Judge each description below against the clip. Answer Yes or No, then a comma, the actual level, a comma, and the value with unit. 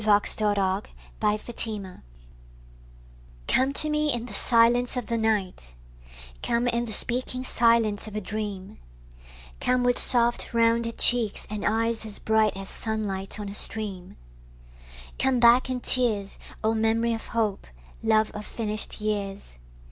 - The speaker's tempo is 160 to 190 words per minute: No, average, 140 wpm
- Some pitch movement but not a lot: No, narrow, 2.2 semitones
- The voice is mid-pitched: No, high, 220 Hz